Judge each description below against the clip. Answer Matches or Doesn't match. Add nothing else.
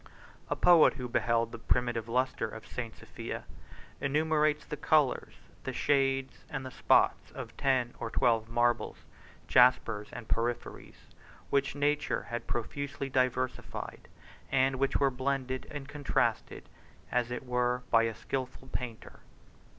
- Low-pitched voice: Matches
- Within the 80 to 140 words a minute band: Matches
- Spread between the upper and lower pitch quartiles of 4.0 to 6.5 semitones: Doesn't match